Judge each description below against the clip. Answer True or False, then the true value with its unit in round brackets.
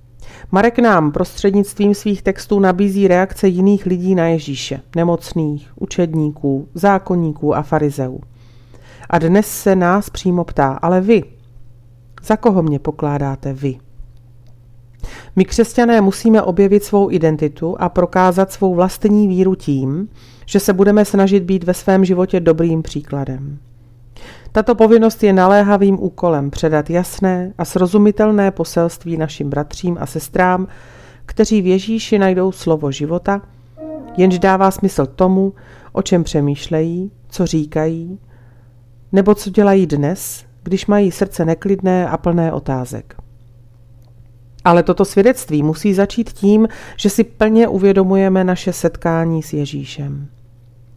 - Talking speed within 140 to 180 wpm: False (125 wpm)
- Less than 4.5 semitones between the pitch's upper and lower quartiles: False (5.7 semitones)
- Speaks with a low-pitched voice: False (175 Hz)